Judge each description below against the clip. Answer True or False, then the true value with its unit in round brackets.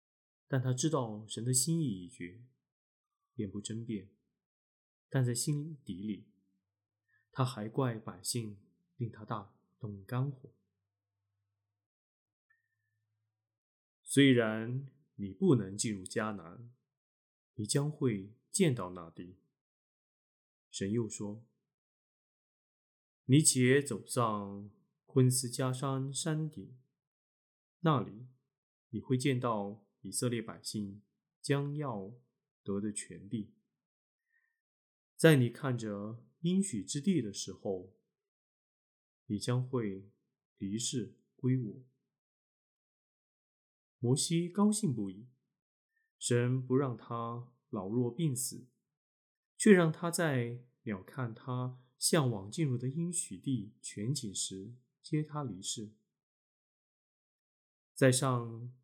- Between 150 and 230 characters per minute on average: False (135 characters per minute)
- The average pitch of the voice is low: True (120 Hz)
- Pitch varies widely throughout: False (5.0 semitones)